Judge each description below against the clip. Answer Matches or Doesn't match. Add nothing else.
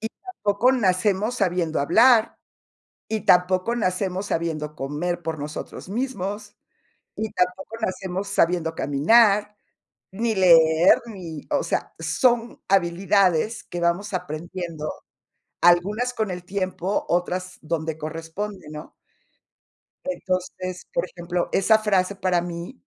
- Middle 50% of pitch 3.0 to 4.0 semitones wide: Matches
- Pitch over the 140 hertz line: Matches